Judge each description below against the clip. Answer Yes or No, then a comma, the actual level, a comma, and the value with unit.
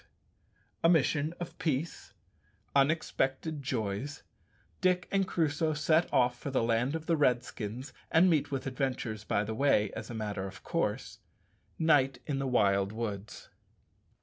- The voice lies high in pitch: No, low, 135 Hz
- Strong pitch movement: Yes, wide, 5.7 semitones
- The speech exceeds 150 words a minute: No, average, 145 wpm